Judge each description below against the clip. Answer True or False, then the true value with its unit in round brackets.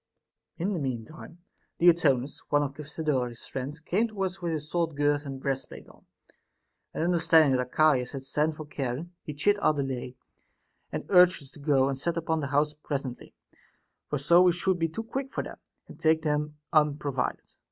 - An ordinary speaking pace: True (185 wpm)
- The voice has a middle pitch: True (150 Hz)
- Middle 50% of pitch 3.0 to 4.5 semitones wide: True (3.4 semitones)